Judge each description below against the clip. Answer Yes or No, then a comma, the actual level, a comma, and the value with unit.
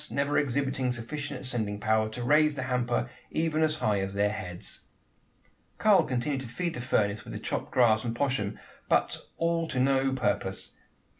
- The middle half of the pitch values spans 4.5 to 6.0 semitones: Yes, average, 4.9 semitones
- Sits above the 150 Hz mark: No, low, 125 Hz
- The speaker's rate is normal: Yes, average, 170 wpm